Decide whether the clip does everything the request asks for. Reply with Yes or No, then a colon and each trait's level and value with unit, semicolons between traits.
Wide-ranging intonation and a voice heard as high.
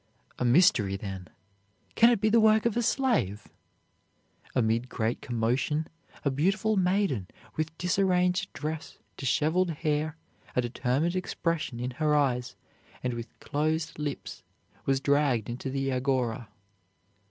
No: wide, 6.4 semitones; medium, 145 Hz